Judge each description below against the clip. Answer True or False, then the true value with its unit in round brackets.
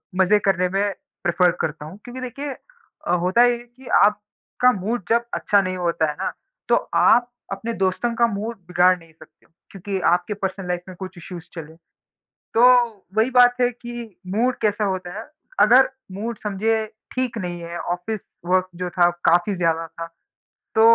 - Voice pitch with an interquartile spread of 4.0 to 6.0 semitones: True (4.8 semitones)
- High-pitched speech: True (195 Hz)